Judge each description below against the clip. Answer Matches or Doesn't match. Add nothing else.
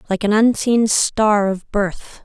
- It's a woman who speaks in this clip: Matches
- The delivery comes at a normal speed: Matches